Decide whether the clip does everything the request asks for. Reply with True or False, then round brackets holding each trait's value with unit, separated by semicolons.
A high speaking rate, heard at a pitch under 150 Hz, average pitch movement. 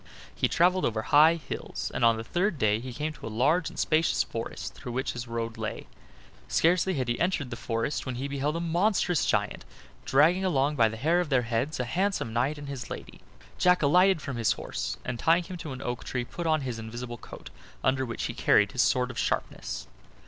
False (220 wpm; 135 Hz; 5.7 semitones)